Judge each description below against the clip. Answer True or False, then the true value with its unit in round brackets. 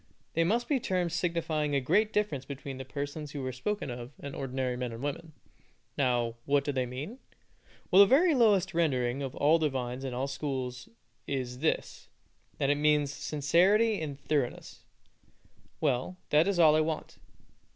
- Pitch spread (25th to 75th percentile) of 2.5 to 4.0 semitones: False (4.4 semitones)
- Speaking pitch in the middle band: True (145 Hz)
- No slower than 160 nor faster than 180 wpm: True (170 wpm)